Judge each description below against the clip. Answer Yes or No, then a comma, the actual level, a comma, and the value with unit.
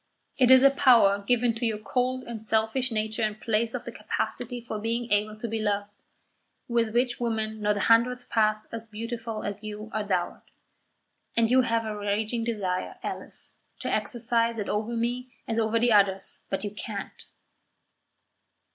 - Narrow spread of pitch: Yes, narrow, 2.0 semitones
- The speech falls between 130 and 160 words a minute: No, average, 175 wpm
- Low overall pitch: No, high, 225 Hz